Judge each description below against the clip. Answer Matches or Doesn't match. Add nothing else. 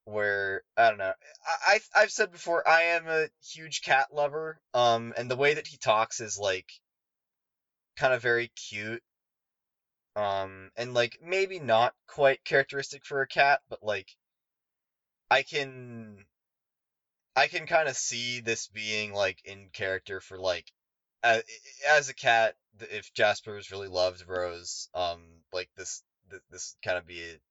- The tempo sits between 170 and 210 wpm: Doesn't match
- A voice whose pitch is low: Matches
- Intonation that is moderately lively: Doesn't match